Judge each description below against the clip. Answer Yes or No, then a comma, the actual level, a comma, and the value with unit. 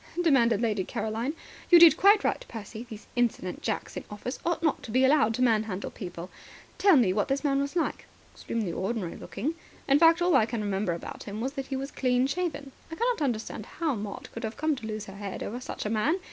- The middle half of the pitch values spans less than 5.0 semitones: No, average, 5.3 semitones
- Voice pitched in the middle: No, high, 245 Hz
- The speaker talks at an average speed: No, fast, 225 wpm